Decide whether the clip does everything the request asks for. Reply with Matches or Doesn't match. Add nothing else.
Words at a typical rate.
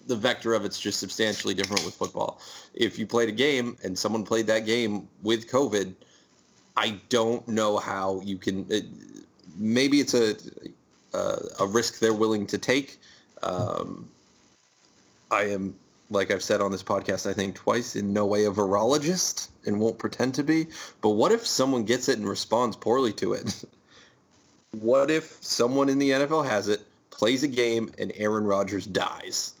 Matches